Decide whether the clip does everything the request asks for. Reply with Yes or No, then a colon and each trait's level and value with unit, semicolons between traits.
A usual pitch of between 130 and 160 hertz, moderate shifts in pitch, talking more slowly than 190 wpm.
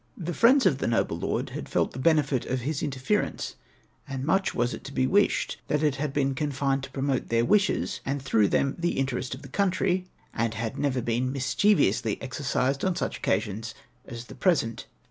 No: low, 135 Hz; average, 3.6 semitones; fast, 205 wpm